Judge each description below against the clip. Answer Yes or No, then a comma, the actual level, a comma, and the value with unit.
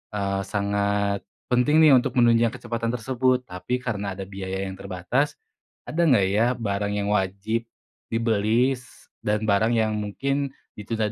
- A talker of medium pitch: No, low, 110 Hz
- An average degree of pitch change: Yes, average, 3.2 semitones